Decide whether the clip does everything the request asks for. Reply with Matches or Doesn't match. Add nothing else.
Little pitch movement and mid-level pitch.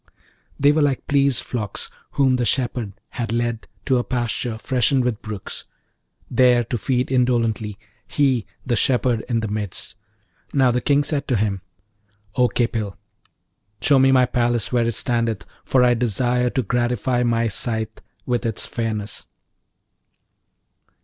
Doesn't match